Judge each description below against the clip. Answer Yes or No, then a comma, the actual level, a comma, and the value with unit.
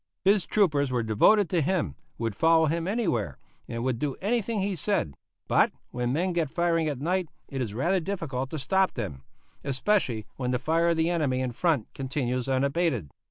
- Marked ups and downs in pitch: Yes, wide, 5.7 semitones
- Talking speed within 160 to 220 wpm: Yes, average, 185 wpm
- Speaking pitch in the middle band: Yes, medium, 150 Hz